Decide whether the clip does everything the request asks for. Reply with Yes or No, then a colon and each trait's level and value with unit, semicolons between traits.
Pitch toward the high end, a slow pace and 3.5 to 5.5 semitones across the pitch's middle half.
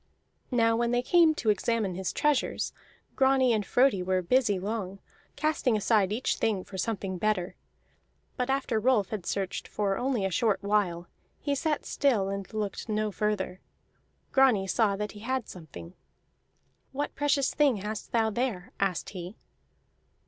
No: high, 215 Hz; average, 155 wpm; average, 4.6 semitones